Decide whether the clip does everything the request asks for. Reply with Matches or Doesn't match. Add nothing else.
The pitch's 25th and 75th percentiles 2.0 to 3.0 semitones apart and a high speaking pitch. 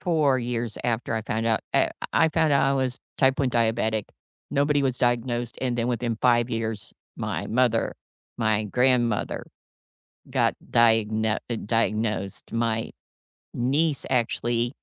Doesn't match